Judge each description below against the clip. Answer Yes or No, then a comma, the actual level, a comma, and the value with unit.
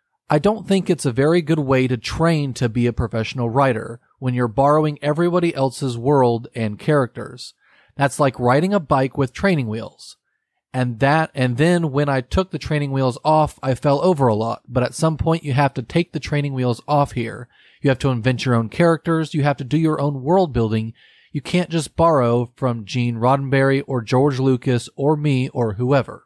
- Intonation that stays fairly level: No, average, 3.8 semitones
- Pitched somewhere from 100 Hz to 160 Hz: Yes, low, 135 Hz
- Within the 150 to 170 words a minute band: No, fast, 205 wpm